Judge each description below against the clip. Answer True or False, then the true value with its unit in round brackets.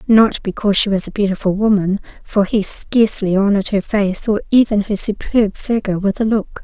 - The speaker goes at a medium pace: True (190 wpm)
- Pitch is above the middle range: True (205 Hz)